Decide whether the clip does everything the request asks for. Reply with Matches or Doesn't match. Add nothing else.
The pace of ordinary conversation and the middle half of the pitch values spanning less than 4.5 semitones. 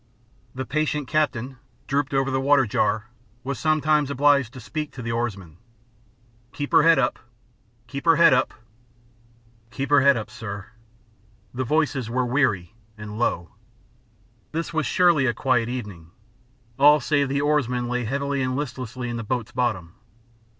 Matches